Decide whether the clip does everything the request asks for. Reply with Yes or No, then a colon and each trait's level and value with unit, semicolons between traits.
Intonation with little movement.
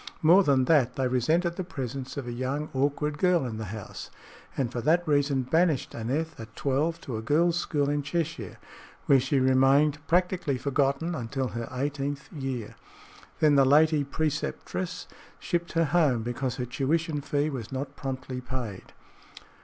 No: average, 3.5 semitones